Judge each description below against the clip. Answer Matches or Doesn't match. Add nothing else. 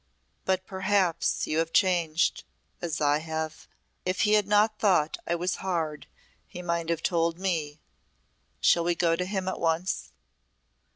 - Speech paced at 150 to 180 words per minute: Matches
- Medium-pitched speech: Matches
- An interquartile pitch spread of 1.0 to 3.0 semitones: Matches